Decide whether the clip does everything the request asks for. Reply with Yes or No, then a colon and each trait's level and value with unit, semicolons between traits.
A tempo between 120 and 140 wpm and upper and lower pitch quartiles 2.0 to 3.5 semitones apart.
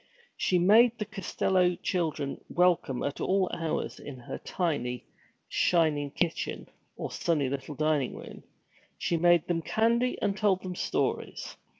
No: slow, 135 wpm; average, 4.3 semitones